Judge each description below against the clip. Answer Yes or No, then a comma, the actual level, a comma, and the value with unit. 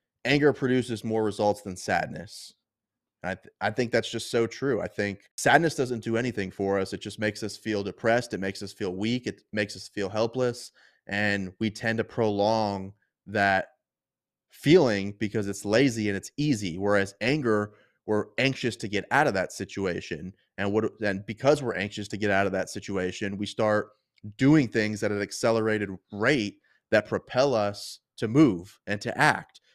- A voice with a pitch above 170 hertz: No, low, 105 Hz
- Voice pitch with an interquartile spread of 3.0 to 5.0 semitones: No, narrow, 2.4 semitones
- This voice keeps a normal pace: Yes, average, 180 wpm